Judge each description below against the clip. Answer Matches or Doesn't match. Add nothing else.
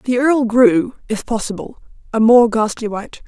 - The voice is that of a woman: Matches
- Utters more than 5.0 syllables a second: Doesn't match